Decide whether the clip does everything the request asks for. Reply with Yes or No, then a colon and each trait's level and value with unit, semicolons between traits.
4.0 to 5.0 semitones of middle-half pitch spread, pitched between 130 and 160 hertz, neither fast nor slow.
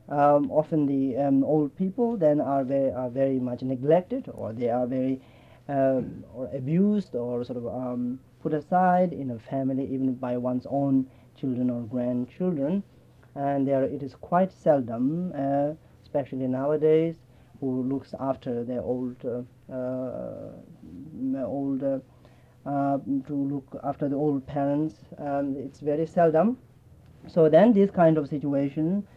No: average, 3.3 semitones; low, 135 Hz; average, 145 wpm